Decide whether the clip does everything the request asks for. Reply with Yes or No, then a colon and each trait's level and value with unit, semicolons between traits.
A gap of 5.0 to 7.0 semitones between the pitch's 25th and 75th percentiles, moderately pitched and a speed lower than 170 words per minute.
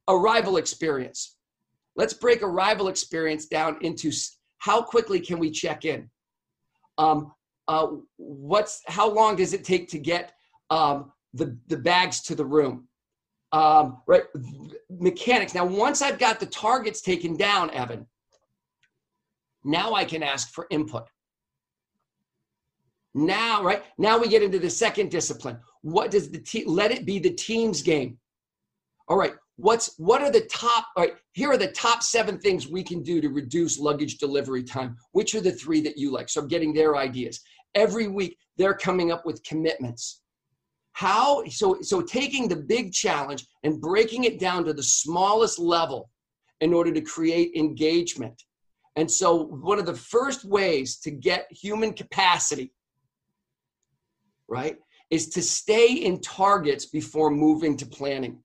Yes: wide, 5.4 semitones; medium, 170 Hz; average, 155 wpm